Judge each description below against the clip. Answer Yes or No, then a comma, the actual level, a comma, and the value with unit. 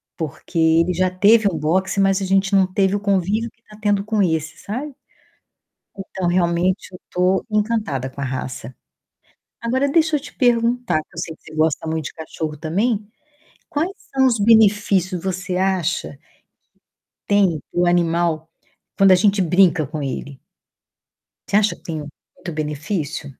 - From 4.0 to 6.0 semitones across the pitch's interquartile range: Yes, average, 4.3 semitones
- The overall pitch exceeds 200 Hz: No, medium, 185 Hz